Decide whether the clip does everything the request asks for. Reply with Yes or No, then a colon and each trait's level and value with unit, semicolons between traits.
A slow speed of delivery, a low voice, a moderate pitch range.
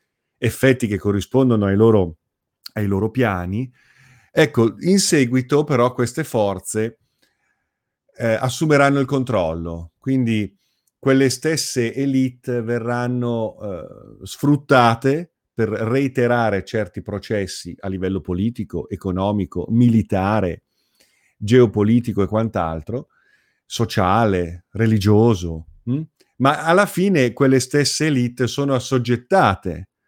Yes: slow, 95 wpm; low, 115 Hz; average, 4.6 semitones